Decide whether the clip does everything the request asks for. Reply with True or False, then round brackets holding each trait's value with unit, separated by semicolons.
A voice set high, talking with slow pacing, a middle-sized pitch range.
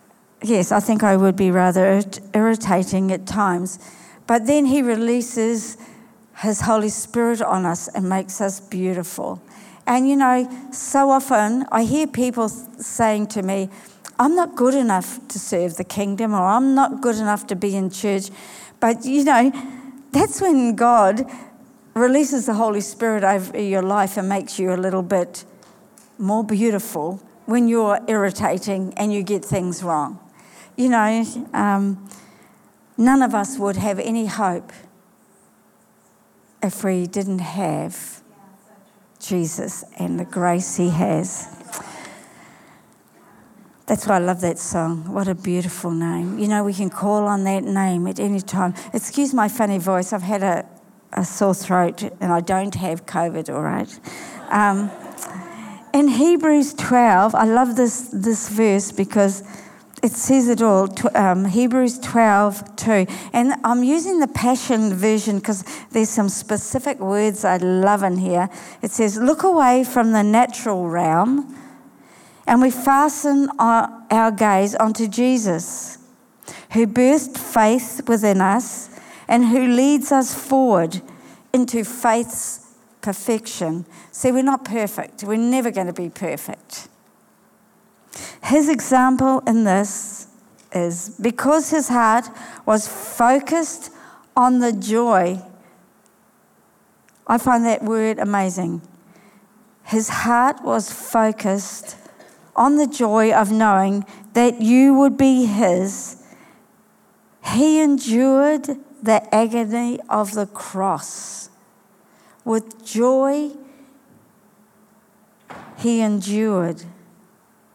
True (215 Hz; 130 wpm; 3.9 semitones)